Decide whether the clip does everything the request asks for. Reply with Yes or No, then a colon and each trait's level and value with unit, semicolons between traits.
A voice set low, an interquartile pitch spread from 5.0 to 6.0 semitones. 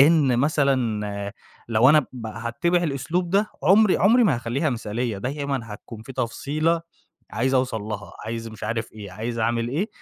Yes: low, 125 Hz; average, 5.3 semitones